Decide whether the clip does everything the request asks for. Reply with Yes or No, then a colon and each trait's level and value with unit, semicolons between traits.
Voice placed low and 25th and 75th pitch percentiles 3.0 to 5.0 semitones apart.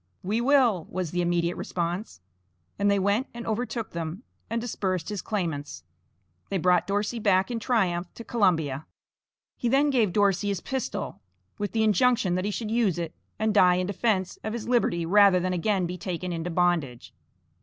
No: high, 195 Hz; average, 4.0 semitones